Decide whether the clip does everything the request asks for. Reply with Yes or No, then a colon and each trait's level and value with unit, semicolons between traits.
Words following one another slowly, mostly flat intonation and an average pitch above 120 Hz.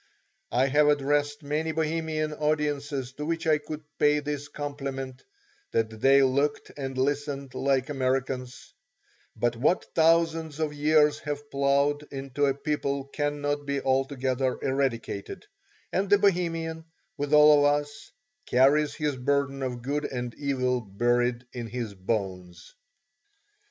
Yes: slow, 130 wpm; narrow, 2.3 semitones; medium, 140 Hz